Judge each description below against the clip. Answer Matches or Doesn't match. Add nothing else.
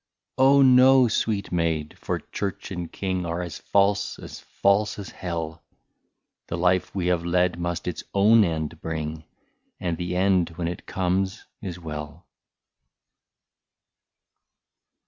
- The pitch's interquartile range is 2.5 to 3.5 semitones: Matches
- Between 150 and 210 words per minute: Doesn't match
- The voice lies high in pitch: Doesn't match